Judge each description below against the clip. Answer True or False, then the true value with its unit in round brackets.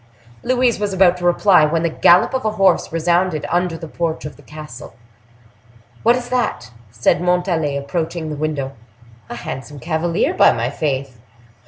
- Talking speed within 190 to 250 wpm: False (165 wpm)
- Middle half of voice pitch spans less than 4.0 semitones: True (3.4 semitones)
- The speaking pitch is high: False (165 Hz)